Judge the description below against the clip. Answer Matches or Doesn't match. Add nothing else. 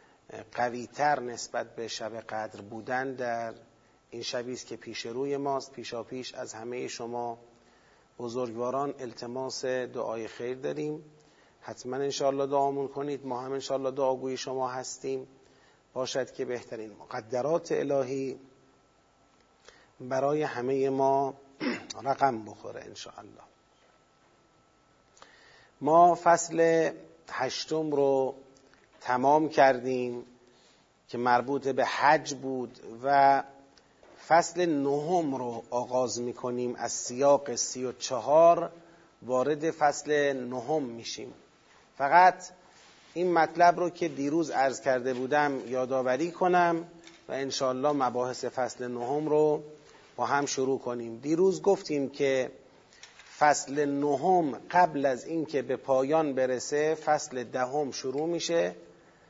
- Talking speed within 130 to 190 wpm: Doesn't match